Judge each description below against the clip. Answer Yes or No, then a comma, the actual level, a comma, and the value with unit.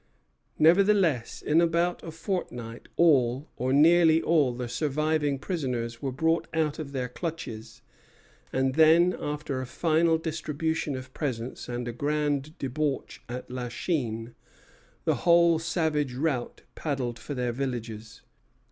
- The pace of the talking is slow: Yes, slow, 130 wpm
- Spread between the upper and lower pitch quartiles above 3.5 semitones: Yes, average, 4.5 semitones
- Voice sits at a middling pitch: Yes, medium, 145 Hz